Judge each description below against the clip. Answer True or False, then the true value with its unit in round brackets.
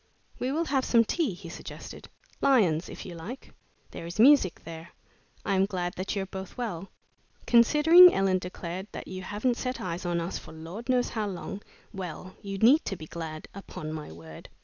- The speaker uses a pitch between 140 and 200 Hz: True (190 Hz)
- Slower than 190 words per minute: False (195 wpm)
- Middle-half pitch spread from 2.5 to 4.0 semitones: False (5.6 semitones)